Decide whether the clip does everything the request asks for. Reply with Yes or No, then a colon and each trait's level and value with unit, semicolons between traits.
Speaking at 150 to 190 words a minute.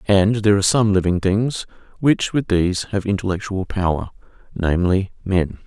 No: average, 140 wpm